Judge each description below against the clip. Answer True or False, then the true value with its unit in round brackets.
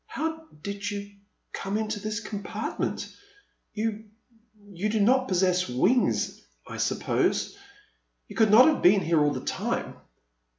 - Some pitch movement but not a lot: False (2.3 semitones)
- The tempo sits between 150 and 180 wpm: False (140 wpm)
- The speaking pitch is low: False (210 Hz)